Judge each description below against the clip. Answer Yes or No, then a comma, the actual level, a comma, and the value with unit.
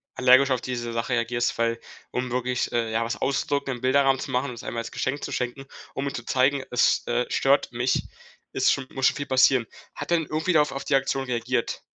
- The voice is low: Yes, low, 130 Hz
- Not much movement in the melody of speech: Yes, narrow, 2.2 semitones